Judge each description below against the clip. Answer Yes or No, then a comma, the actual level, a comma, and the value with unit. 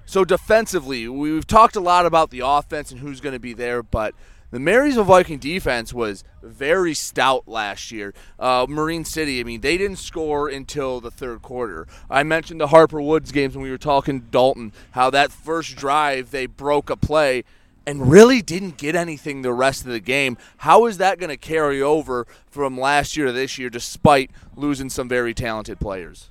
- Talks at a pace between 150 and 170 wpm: No, average, 195 wpm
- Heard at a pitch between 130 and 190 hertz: Yes, medium, 140 Hz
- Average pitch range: Yes, average, 3.8 semitones